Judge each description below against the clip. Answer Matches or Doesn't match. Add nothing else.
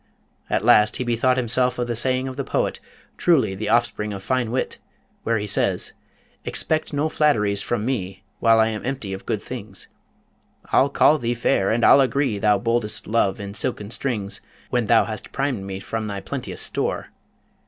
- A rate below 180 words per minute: Doesn't match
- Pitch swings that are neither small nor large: Matches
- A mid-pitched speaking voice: Doesn't match